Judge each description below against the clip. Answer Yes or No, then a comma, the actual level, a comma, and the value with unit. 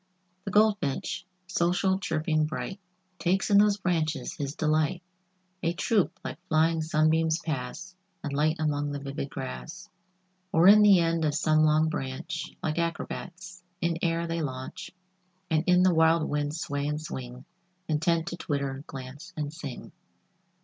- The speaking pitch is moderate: Yes, medium, 160 Hz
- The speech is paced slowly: No, average, 150 wpm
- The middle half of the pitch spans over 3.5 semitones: No, average, 3.0 semitones